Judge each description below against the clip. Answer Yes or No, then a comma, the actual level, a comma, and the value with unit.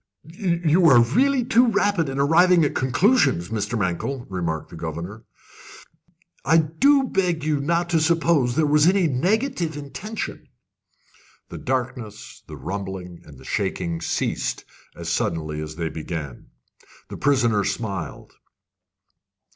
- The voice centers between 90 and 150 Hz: Yes, medium, 140 Hz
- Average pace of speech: No, slow, 130 wpm